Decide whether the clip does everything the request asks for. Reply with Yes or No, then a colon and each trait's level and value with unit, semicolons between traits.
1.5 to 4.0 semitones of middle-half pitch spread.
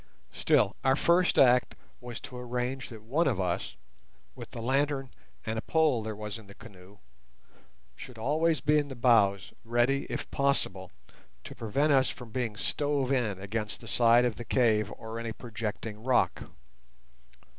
Yes: average, 3.7 semitones